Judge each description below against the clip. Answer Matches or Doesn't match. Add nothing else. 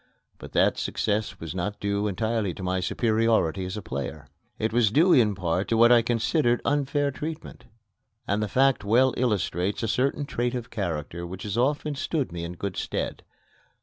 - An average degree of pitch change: Matches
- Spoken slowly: Doesn't match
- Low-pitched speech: Matches